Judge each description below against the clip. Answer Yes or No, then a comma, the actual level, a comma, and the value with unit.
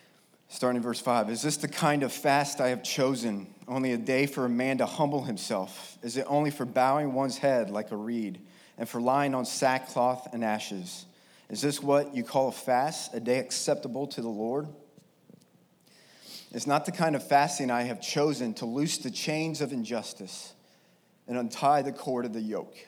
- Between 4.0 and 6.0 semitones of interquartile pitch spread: No, average, 3.4 semitones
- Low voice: Yes, low, 130 Hz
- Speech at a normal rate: Yes, average, 195 wpm